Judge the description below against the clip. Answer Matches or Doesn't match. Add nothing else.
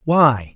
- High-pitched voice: Doesn't match